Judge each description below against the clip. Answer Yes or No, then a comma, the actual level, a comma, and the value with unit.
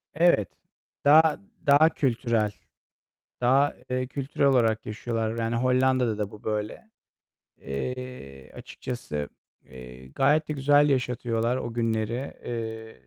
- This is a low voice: Yes, low, 120 Hz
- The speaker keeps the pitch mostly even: No, average, 3.5 semitones